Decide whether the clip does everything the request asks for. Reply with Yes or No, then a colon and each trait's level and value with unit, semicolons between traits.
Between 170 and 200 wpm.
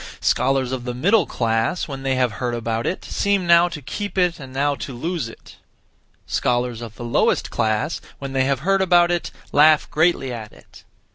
Yes: average, 195 wpm